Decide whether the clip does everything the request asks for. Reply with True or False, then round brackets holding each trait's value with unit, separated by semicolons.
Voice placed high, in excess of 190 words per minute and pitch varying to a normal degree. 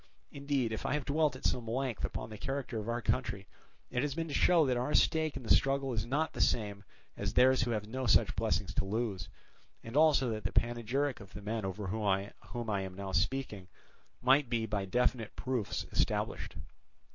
False (120 Hz; 205 wpm; 4.4 semitones)